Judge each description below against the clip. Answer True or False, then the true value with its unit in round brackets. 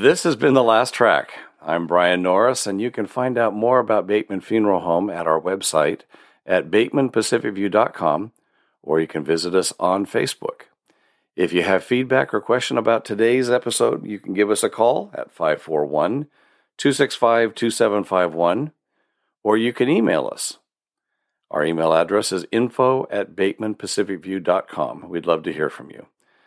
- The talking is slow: False (150 wpm)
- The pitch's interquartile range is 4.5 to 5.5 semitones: True (4.8 semitones)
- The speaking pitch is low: True (105 Hz)